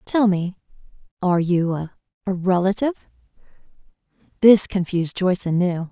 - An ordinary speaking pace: No, slow, 100 wpm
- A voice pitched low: No, medium, 185 Hz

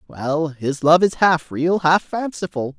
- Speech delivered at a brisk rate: No, average, 170 wpm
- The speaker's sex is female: No, male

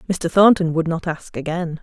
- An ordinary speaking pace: Yes, average, 195 wpm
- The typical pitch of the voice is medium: Yes, medium, 170 Hz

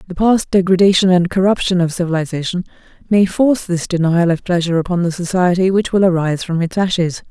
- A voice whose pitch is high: No, medium, 180 Hz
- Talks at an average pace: Yes, average, 180 wpm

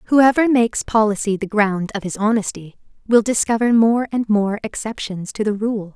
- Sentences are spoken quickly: No, average, 170 wpm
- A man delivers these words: No, female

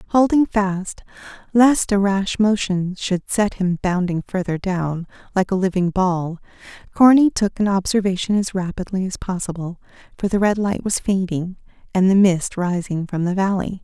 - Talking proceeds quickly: No, average, 160 wpm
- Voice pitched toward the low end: No, high, 190 Hz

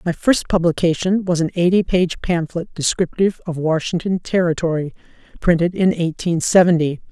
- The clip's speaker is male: No, female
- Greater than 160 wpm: No, slow, 135 wpm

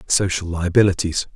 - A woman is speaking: No, male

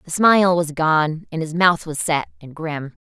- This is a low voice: No, medium, 165 Hz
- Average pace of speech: No, fast, 220 wpm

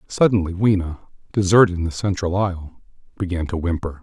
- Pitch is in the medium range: No, very low, 90 Hz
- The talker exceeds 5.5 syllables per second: Yes, 5.8 syllables/s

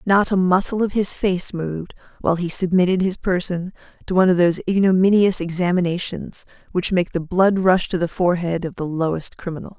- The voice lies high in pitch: No, medium, 180 Hz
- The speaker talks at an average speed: Yes, average, 185 wpm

